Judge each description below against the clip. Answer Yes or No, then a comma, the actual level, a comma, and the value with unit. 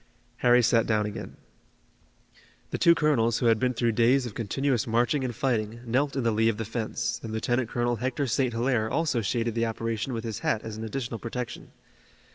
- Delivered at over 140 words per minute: Yes, average, 200 wpm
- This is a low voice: Yes, low, 115 Hz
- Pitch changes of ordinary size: No, narrow, 2.1 semitones